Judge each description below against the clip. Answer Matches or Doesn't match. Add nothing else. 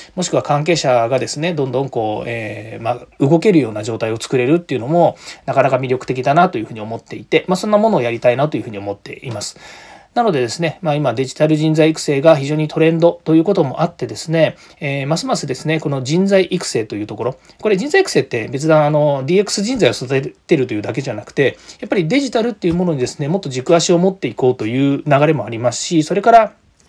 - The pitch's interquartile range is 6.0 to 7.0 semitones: Doesn't match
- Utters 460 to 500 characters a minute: Matches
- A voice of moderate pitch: Matches